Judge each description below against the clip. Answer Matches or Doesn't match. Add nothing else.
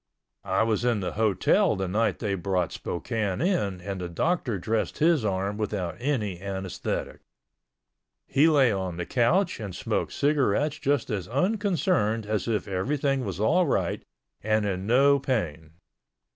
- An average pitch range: Doesn't match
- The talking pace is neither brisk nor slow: Matches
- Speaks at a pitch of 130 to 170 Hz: Doesn't match